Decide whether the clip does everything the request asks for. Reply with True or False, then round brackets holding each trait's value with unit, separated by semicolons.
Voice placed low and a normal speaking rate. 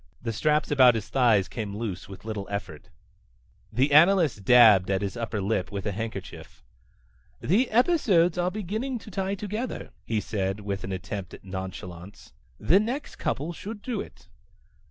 True (115 Hz; 160 wpm)